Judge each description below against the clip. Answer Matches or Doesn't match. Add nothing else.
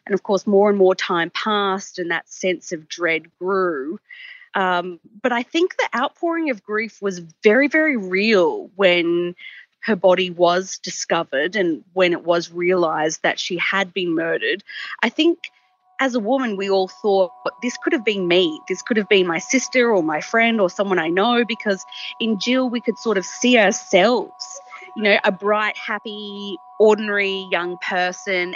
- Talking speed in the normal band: Matches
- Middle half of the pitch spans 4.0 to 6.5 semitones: Matches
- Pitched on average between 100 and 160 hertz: Doesn't match